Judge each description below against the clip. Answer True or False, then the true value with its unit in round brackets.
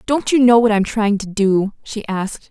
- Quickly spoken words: True (240 wpm)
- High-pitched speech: True (215 Hz)